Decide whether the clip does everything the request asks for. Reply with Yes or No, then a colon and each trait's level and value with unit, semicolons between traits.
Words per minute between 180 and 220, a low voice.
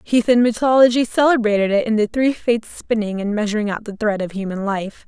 No: average, 200 wpm; high, 220 Hz